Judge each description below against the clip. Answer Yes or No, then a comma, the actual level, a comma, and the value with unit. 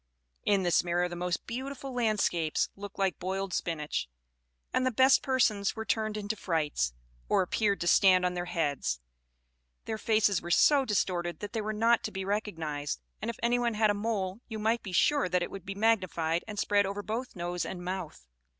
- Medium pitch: No, high, 200 Hz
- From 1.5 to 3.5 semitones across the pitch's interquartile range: No, average, 3.9 semitones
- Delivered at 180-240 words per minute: Yes, average, 195 wpm